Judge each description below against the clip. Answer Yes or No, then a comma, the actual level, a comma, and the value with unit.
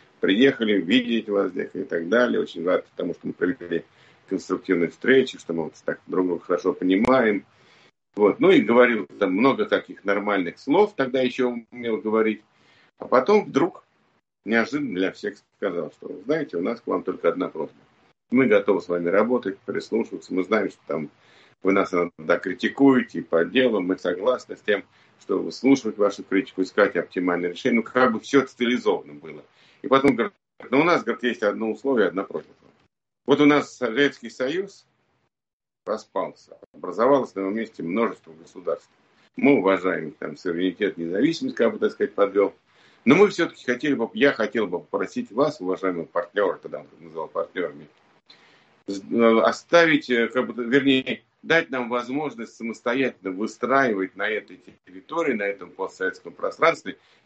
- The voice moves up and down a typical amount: No, wide, 6.1 semitones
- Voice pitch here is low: Yes, low, 120 Hz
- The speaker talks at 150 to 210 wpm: Yes, fast, 160 wpm